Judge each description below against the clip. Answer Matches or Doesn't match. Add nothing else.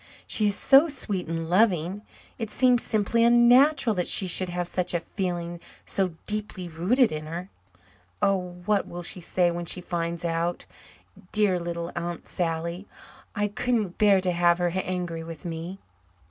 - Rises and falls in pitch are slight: Doesn't match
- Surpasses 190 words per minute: Doesn't match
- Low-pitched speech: Doesn't match